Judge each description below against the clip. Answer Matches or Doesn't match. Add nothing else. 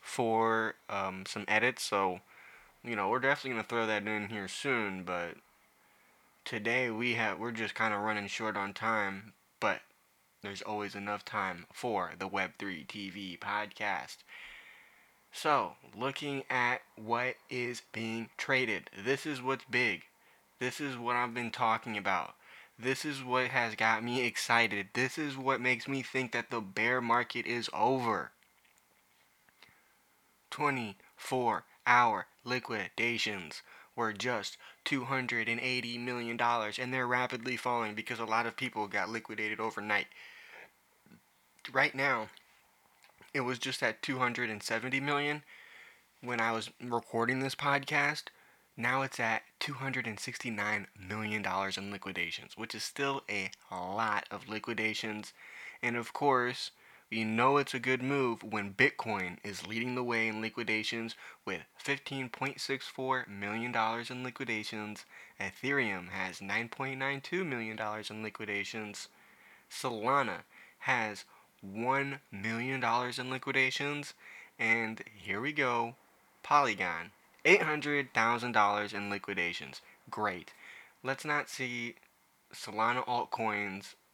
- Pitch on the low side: Matches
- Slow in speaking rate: Matches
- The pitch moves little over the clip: Doesn't match